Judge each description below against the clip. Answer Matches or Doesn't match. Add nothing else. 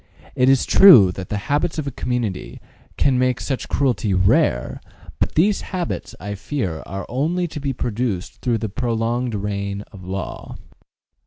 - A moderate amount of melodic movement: Doesn't match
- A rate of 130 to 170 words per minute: Matches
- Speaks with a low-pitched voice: Matches